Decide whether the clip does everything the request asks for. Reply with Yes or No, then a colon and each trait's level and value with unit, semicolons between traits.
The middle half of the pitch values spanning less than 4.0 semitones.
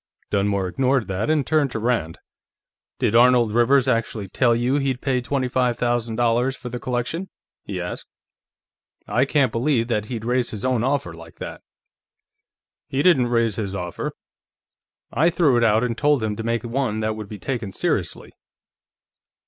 Yes: average, 3.1 semitones